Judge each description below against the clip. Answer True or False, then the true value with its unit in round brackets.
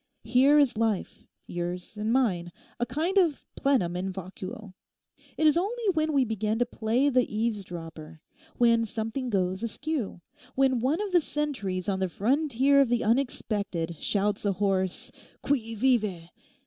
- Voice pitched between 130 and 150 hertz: False (225 Hz)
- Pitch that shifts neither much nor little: False (6.2 semitones)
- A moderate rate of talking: True (145 wpm)